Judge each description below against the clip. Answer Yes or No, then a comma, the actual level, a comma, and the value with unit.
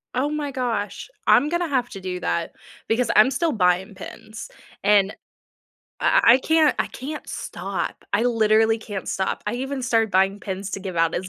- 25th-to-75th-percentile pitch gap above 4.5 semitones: Yes, average, 4.9 semitones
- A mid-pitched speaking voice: No, high, 220 Hz